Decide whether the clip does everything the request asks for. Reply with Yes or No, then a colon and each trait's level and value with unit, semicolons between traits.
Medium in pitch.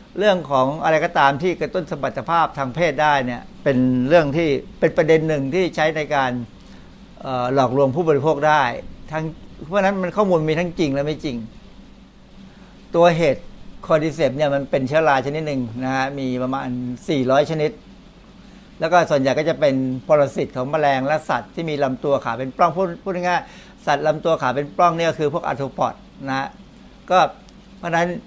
Yes: medium, 155 Hz